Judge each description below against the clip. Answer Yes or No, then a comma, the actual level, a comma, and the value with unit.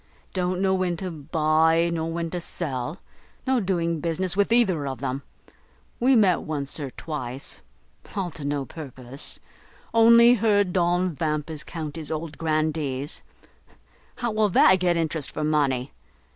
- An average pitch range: Yes, average, 3.7 semitones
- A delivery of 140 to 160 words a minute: Yes, average, 145 wpm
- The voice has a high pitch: No, medium, 165 Hz